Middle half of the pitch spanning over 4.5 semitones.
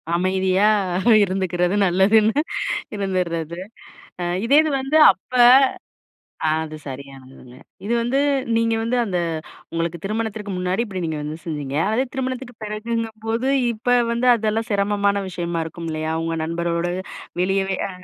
Yes: average, 4.9 semitones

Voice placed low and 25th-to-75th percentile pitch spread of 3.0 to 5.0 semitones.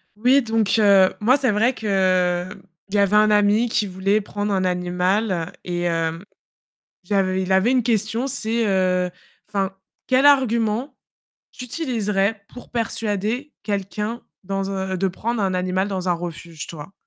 No: high, 200 Hz; average, 3.3 semitones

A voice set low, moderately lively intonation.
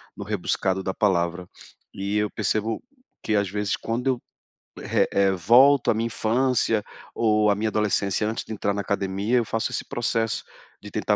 No: low, 105 Hz; narrow, 2.3 semitones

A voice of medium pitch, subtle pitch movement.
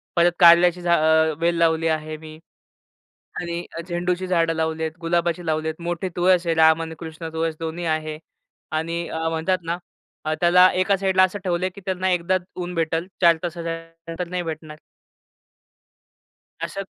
Yes: medium, 170 Hz; narrow, 1.7 semitones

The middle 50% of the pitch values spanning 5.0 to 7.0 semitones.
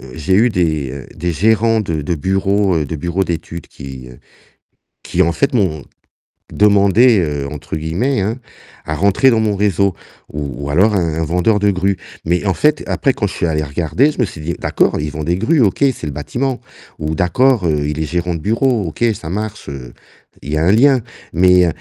Yes: wide, 5.5 semitones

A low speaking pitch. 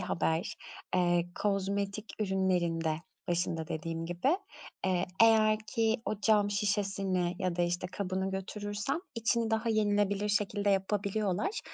No: high, 195 Hz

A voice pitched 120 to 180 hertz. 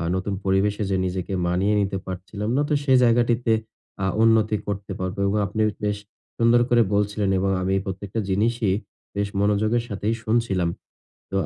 No: low, 105 Hz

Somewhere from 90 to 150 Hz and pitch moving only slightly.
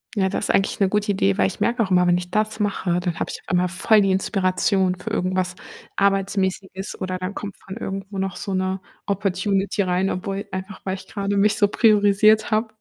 No: high, 195 Hz; narrow, 1.7 semitones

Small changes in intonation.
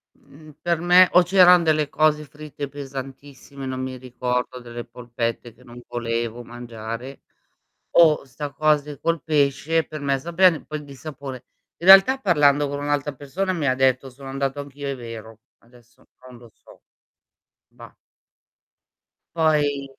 No: average, 3.5 semitones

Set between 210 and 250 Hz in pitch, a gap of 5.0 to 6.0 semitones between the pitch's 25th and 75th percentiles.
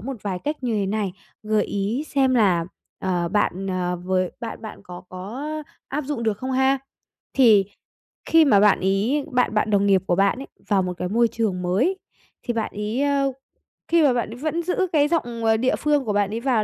Yes: high, 225 Hz; wide, 5.5 semitones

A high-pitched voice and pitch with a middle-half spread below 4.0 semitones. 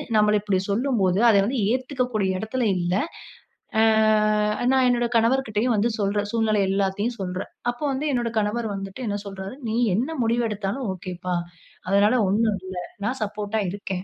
Yes: high, 210 Hz; average, 3.4 semitones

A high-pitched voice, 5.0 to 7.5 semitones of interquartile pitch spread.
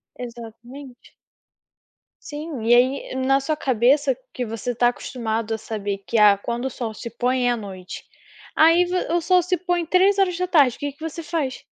Yes: very high, 255 Hz; wide, 5.5 semitones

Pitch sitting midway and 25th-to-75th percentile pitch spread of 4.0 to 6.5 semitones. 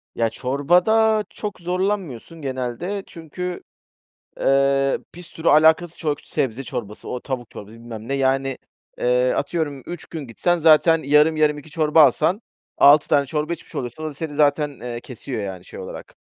Yes: medium, 150 Hz; average, 4.3 semitones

